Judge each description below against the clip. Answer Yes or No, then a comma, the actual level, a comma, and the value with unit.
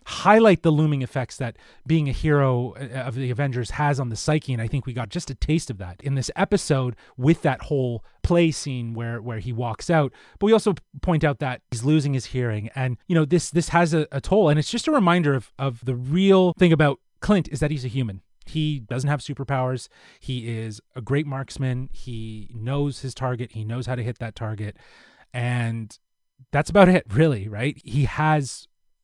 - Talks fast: Yes, fast, 210 wpm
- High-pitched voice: No, low, 135 Hz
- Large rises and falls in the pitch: No, average, 4.1 semitones